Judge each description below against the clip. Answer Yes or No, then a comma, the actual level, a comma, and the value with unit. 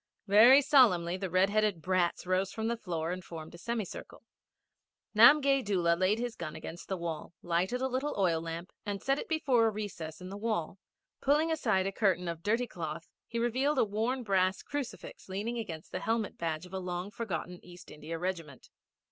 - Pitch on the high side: Yes, high, 195 Hz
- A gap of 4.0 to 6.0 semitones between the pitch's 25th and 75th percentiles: Yes, average, 5.2 semitones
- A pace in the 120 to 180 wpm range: No, average, 190 wpm